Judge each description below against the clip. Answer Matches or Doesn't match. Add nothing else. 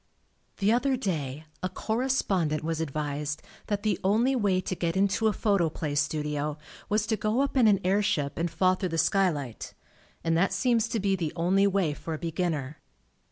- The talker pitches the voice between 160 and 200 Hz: Matches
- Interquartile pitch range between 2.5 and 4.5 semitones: Doesn't match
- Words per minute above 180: Matches